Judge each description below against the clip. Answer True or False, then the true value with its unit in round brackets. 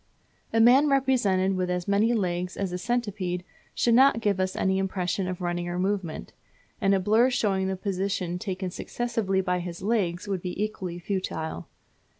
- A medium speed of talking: True (170 wpm)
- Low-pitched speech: False (190 Hz)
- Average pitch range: True (3.0 semitones)